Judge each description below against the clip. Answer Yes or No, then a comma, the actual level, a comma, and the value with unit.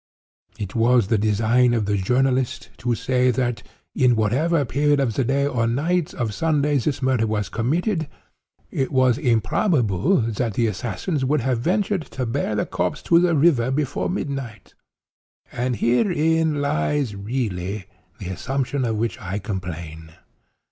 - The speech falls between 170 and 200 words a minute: No, average, 150 wpm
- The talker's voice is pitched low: Yes, low, 125 Hz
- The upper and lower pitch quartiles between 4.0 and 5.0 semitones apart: Yes, average, 4.7 semitones